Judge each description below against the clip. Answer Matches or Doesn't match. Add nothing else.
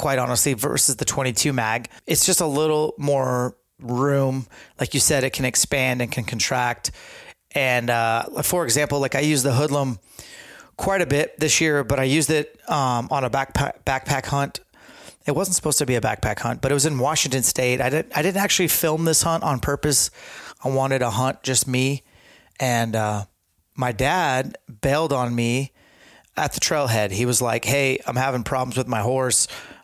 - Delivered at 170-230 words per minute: Matches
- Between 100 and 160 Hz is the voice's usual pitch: Matches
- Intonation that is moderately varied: Matches